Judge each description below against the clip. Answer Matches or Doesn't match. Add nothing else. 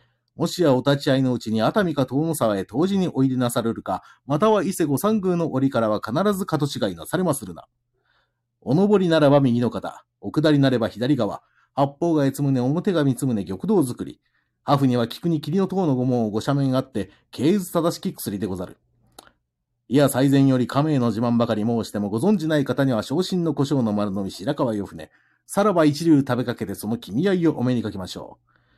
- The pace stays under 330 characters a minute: Doesn't match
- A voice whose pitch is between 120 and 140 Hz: Matches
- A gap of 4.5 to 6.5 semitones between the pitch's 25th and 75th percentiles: Matches